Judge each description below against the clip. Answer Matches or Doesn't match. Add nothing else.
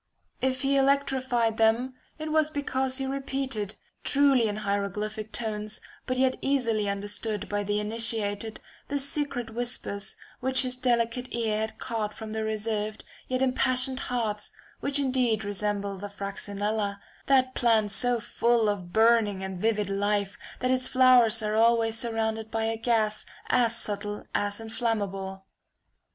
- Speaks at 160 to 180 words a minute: Doesn't match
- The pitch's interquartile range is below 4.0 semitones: Matches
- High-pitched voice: Matches